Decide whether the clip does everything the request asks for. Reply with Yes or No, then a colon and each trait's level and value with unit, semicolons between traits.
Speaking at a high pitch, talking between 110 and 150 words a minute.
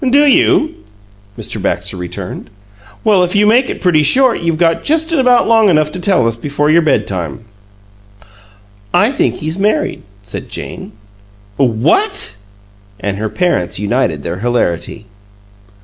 No: medium, 165 Hz; average, 140 wpm